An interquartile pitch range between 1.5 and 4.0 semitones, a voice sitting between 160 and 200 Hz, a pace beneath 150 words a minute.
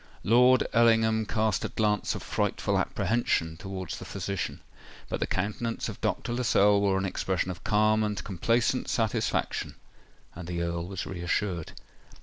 No: average, 3.5 semitones; low, 105 Hz; average, 140 wpm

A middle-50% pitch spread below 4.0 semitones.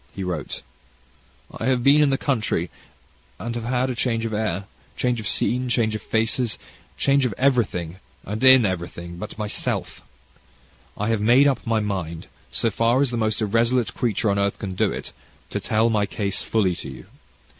Yes: average, 3.6 semitones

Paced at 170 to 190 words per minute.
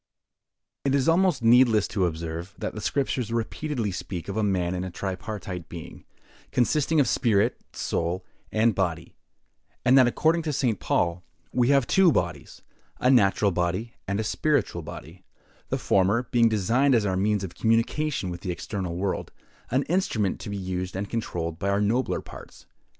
No: average, 160 wpm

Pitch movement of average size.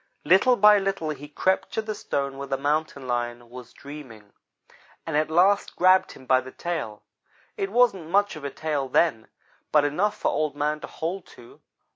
No: wide, 5.7 semitones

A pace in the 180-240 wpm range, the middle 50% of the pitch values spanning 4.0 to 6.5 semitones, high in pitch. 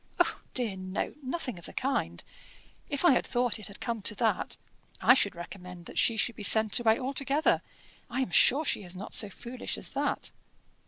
Yes: average, 195 wpm; average, 4.7 semitones; high, 230 Hz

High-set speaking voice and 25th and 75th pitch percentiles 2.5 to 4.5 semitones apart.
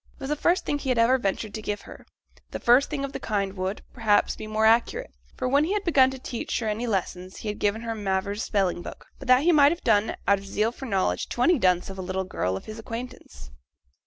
No: high, 220 Hz; average, 5.0 semitones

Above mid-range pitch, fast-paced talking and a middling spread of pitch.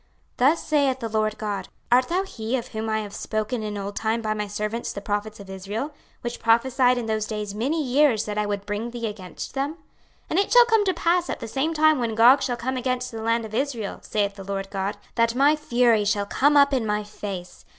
Yes: high, 225 Hz; fast, 240 wpm; average, 4.1 semitones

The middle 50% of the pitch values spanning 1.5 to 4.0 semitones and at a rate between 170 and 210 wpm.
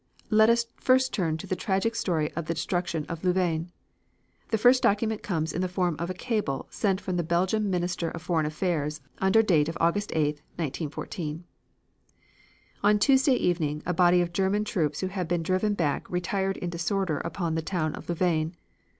Yes: average, 3.3 semitones; average, 180 wpm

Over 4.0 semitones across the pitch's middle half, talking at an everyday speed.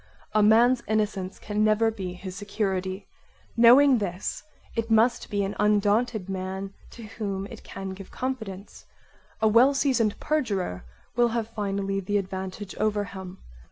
No: average, 2.8 semitones; average, 145 wpm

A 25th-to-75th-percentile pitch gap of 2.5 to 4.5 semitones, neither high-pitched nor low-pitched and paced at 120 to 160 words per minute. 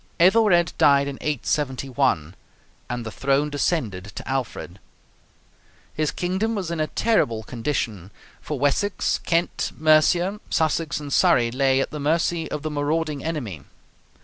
Yes: average, 4.0 semitones; medium, 150 Hz; slow, 135 wpm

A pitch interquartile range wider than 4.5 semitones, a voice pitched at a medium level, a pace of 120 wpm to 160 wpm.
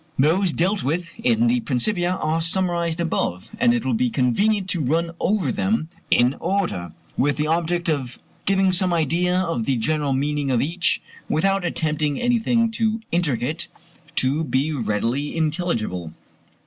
Yes: average, 5.0 semitones; medium, 165 Hz; average, 150 wpm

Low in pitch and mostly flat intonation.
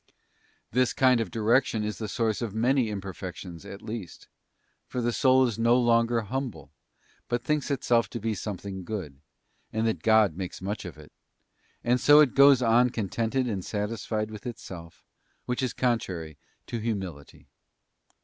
No: low, 115 Hz; average, 3.7 semitones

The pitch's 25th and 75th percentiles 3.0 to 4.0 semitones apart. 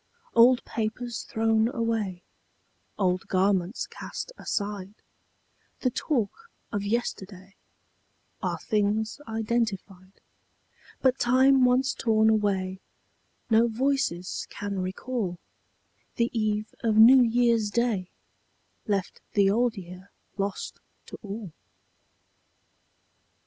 Yes: average, 3.3 semitones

